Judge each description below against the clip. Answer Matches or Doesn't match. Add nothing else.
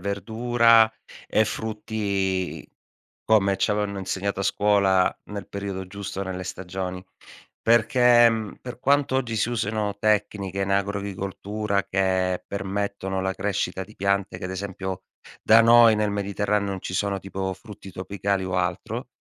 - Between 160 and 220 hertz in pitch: Doesn't match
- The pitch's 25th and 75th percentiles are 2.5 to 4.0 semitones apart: Doesn't match